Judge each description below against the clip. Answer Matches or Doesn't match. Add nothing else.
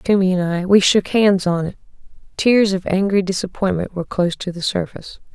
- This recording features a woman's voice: Matches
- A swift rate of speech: Doesn't match